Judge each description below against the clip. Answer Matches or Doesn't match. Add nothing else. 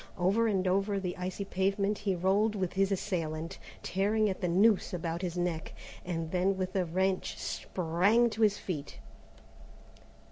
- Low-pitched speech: Doesn't match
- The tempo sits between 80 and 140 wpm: Doesn't match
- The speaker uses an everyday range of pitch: Doesn't match